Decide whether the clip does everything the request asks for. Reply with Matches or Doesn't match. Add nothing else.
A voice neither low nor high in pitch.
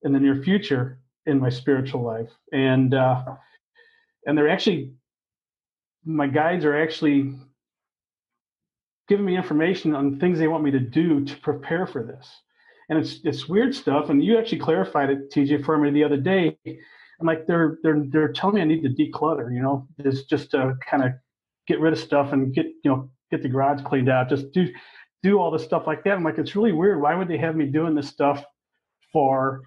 Matches